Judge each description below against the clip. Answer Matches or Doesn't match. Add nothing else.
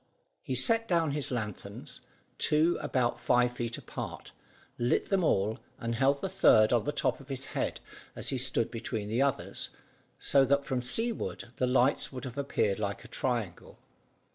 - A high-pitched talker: Doesn't match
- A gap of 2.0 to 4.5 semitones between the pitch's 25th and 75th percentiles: Matches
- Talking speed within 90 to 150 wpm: Doesn't match